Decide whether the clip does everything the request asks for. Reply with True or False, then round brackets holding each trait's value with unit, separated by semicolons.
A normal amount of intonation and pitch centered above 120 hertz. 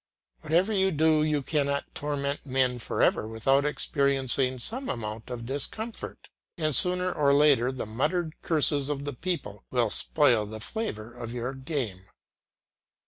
True (4.2 semitones; 140 Hz)